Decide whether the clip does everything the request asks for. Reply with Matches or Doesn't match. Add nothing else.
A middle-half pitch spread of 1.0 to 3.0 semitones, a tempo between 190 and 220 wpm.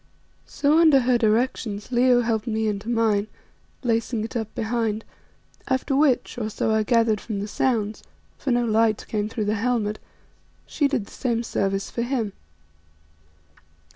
Doesn't match